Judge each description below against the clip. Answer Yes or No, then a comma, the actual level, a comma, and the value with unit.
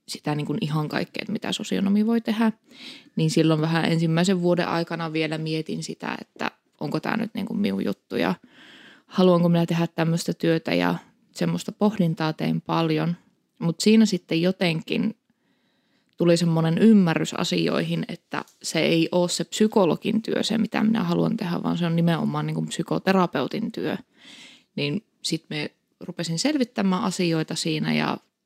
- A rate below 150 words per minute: No, fast, 155 wpm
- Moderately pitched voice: Yes, medium, 175 Hz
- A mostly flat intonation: No, average, 5.2 semitones